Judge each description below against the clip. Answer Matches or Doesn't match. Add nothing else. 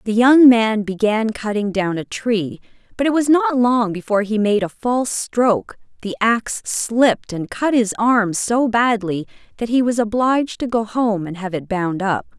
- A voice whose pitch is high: Matches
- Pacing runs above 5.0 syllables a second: Doesn't match